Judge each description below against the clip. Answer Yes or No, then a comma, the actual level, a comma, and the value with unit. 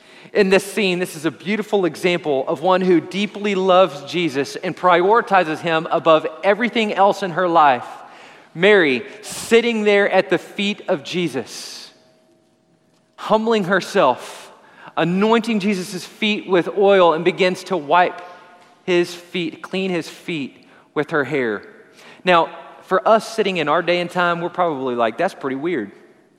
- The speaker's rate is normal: Yes, average, 150 wpm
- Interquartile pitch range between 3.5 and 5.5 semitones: No, average, 2.8 semitones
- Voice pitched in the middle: Yes, medium, 180 Hz